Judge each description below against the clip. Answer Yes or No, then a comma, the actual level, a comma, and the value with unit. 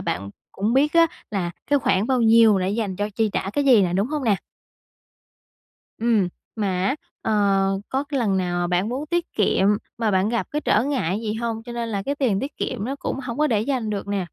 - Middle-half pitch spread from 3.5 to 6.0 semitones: Yes, average, 4.9 semitones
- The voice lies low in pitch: No, high, 220 Hz